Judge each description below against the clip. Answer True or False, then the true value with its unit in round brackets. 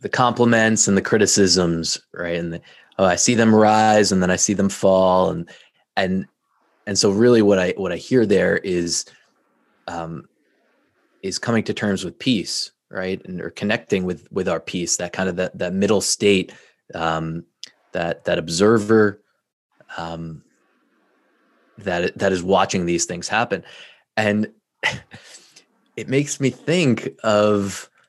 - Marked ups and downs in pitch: False (3.3 semitones)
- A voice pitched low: True (100 Hz)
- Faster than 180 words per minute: False (150 wpm)